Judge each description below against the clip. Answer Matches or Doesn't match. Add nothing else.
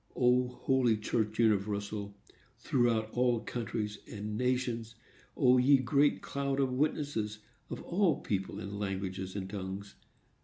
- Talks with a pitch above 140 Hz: Doesn't match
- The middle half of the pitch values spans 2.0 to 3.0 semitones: Doesn't match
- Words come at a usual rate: Doesn't match